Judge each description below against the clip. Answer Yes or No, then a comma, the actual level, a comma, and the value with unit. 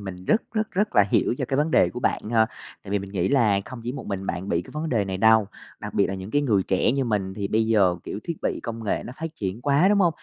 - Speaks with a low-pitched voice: Yes, low, 110 Hz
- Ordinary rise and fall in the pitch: No, wide, 6.2 semitones